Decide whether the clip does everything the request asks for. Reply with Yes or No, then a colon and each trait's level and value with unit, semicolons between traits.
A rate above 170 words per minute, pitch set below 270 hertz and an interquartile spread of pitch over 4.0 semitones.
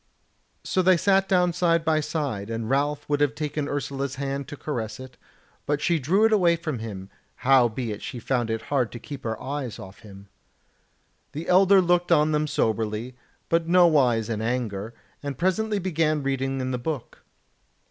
Yes: average, 180 wpm; medium, 140 Hz; wide, 5.5 semitones